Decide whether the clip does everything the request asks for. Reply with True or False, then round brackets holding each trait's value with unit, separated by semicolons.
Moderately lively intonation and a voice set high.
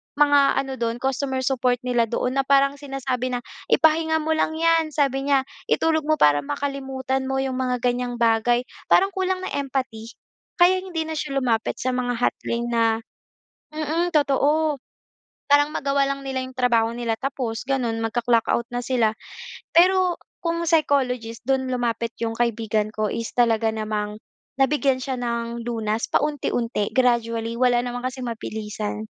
True (3.3 semitones; 255 Hz)